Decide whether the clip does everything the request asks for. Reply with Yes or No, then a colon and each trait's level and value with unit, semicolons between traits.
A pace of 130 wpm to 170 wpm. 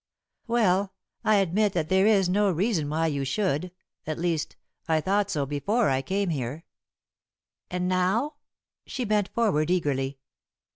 Yes: average, 145 wpm